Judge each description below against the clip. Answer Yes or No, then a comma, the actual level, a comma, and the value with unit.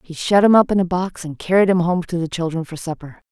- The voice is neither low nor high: Yes, medium, 175 Hz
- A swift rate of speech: Yes, fast, 290 wpm